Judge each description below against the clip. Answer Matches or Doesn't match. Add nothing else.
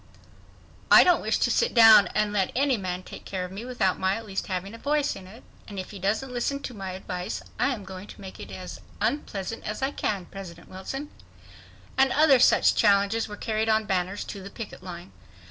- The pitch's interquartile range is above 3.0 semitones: Matches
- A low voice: Doesn't match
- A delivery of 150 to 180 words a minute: Doesn't match